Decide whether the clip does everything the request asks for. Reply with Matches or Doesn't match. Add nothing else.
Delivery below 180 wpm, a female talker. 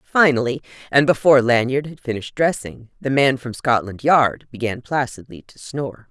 Matches